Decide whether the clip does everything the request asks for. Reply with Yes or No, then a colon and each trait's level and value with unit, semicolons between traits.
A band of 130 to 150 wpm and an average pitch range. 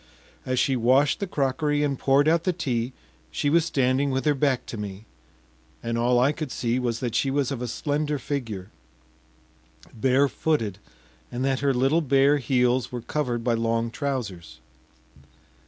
No: average, 165 wpm; average, 3.3 semitones